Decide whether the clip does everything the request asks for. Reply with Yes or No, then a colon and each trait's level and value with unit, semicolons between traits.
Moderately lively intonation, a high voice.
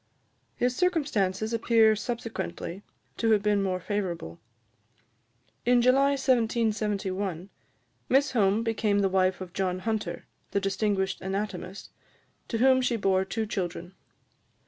Yes: average, 3.4 semitones; high, 210 Hz